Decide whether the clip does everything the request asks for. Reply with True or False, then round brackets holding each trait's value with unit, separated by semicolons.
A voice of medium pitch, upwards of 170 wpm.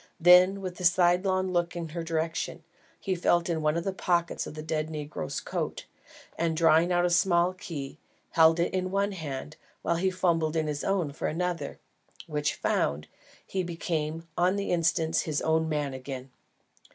True (170 Hz; 180 wpm)